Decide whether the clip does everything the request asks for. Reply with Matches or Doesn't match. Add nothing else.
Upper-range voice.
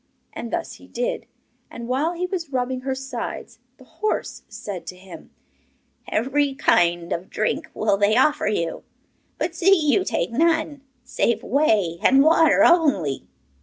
Matches